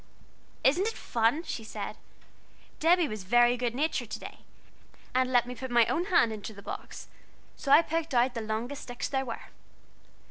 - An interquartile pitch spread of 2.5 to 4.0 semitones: No, average, 4.6 semitones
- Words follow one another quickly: No, average, 180 wpm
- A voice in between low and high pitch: No, very high, 250 Hz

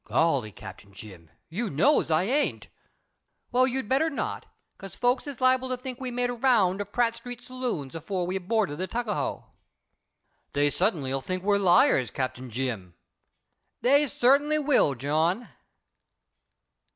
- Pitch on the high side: Yes, high, 205 Hz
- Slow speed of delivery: No, average, 150 wpm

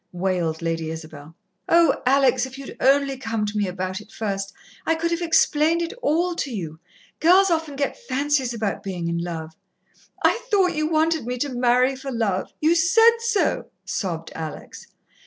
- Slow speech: No, average, 175 wpm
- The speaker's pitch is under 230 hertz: No, very high, 255 Hz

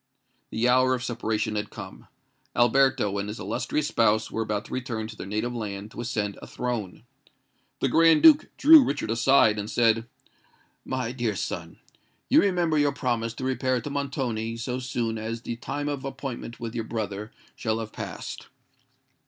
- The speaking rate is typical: Yes, average, 170 wpm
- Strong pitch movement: No, average, 3.2 semitones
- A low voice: Yes, low, 115 Hz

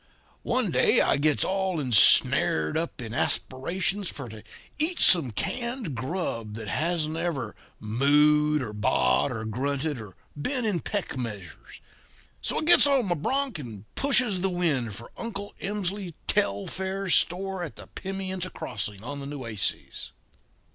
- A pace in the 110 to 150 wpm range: Yes, average, 145 wpm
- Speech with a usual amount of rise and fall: No, wide, 8.4 semitones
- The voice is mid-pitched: Yes, medium, 155 Hz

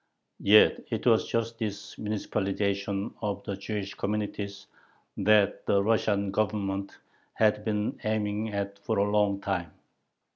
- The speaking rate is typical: No, slow, 130 wpm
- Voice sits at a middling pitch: No, low, 100 Hz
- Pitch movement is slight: Yes, narrow, 1.3 semitones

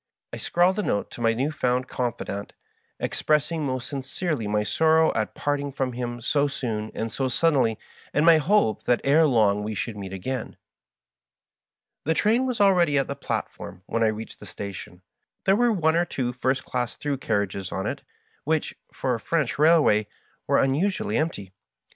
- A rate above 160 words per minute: Yes, average, 180 wpm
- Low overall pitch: Yes, low, 130 Hz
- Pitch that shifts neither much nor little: No, wide, 6.2 semitones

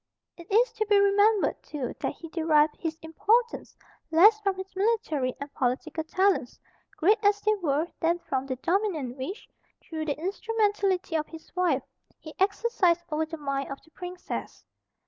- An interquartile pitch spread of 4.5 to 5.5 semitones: Yes, average, 4.8 semitones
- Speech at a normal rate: Yes, average, 165 wpm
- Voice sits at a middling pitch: No, very high, 345 Hz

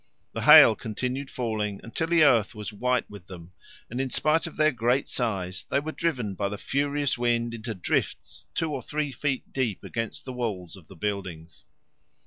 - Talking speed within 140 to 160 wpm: No, average, 185 wpm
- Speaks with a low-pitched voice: Yes, low, 120 Hz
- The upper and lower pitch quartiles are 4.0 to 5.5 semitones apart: Yes, average, 5.1 semitones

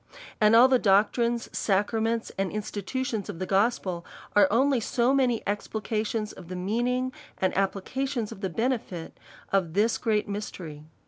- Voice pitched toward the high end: Yes, high, 215 Hz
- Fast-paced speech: No, average, 150 wpm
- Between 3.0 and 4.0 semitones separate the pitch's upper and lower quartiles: Yes, average, 3.5 semitones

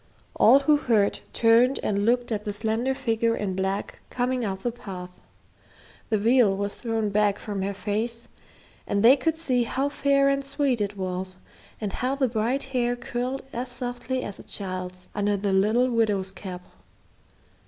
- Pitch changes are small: No, average, 3.9 semitones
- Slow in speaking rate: No, average, 170 wpm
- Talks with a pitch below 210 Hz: No, high, 225 Hz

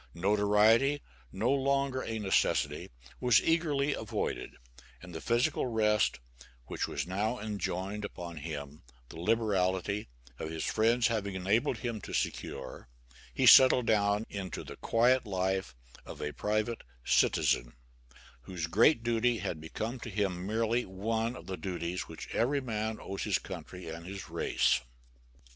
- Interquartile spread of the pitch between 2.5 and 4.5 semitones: Yes, average, 4.1 semitones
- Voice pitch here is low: Yes, low, 105 Hz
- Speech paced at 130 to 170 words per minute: Yes, average, 140 wpm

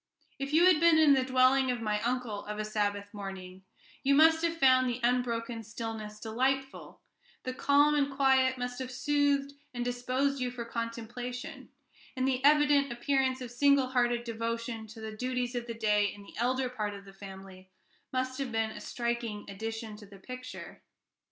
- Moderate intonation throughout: Yes, average, 3.1 semitones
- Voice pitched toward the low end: No, high, 245 Hz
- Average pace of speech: Yes, average, 180 wpm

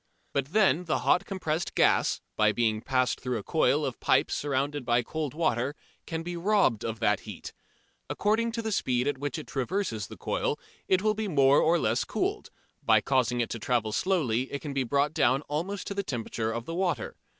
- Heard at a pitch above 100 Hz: Yes, medium, 140 Hz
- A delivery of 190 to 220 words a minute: Yes, fast, 205 wpm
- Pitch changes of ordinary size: No, wide, 6.5 semitones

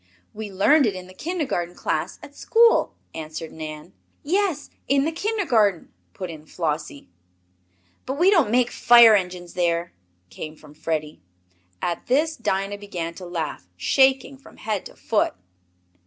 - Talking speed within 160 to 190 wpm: No, average, 145 wpm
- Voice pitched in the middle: No, high, 195 Hz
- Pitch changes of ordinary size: No, wide, 8.4 semitones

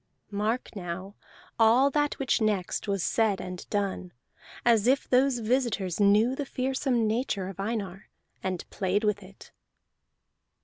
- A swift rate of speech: No, slow, 135 wpm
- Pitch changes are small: No, average, 4.2 semitones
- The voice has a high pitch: Yes, high, 215 Hz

